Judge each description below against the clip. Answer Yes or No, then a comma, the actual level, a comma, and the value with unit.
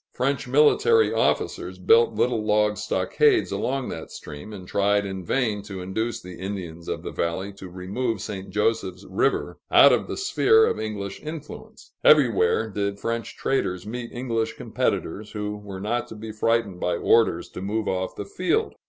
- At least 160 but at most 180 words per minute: Yes, average, 170 wpm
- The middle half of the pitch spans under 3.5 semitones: No, average, 4.3 semitones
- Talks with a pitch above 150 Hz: No, low, 105 Hz